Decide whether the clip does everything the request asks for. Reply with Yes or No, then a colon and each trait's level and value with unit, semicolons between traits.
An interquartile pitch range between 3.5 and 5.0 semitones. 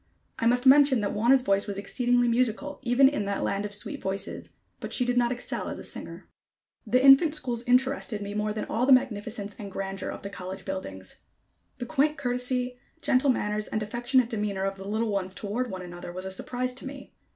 Yes: average, 4.1 semitones